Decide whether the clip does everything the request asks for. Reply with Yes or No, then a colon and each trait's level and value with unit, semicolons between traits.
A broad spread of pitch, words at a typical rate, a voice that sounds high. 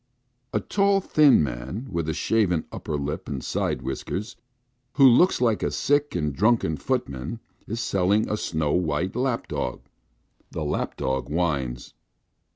No: wide, 8.3 semitones; average, 155 wpm; very low, 90 Hz